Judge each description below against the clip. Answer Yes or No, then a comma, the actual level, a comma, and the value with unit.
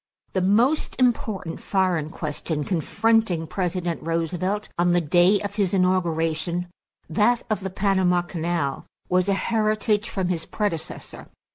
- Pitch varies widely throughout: No, average, 3.4 semitones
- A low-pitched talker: No, medium, 185 Hz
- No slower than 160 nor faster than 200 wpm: No, slow, 135 wpm